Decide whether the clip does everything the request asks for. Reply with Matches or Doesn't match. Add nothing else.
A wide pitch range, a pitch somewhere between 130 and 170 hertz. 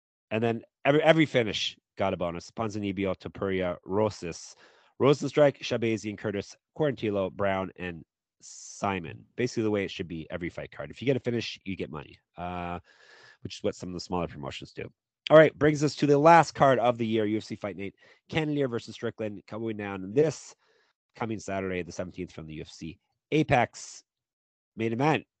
Doesn't match